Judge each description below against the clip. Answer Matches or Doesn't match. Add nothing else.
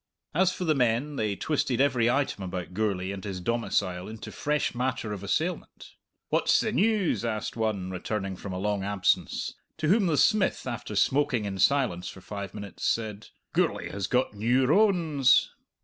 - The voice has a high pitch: Doesn't match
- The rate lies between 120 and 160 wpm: Doesn't match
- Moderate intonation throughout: Doesn't match